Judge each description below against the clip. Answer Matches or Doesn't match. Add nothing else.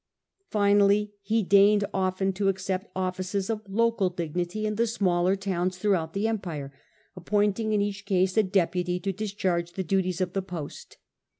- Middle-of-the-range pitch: Doesn't match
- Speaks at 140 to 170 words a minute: Matches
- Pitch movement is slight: Matches